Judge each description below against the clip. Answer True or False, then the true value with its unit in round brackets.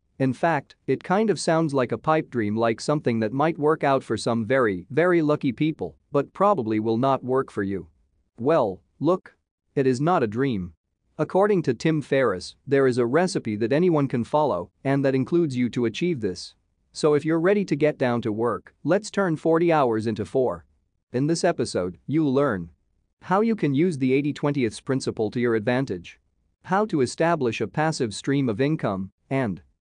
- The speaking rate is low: False (190 wpm)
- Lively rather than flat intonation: True (5.8 semitones)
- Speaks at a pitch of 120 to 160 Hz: True (135 Hz)